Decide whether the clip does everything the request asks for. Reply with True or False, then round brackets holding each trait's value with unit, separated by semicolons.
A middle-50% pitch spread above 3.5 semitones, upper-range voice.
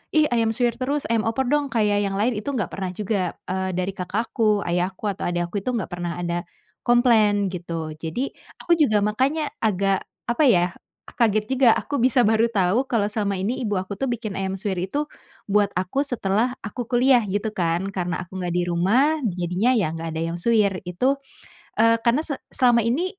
True (4.7 semitones; 210 Hz)